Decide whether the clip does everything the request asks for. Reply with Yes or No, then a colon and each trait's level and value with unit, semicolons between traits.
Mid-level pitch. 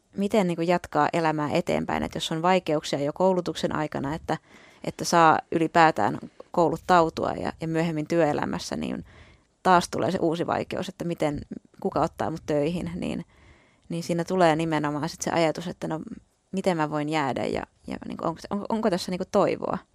Yes: medium, 165 Hz